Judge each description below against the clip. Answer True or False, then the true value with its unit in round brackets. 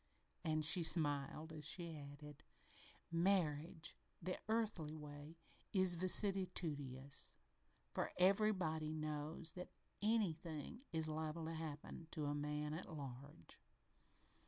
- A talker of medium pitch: True (160 Hz)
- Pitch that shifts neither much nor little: True (3.0 semitones)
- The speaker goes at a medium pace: False (110 wpm)